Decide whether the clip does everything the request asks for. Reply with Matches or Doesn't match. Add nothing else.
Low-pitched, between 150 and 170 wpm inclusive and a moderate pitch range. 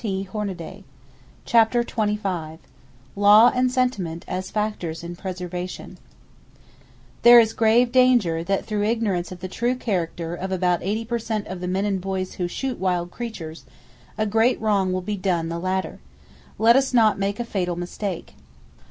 Doesn't match